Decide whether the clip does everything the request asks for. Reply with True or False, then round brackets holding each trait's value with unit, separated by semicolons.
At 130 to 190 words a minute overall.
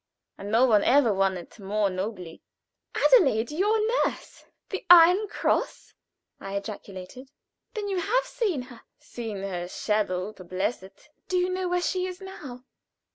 True (155 wpm)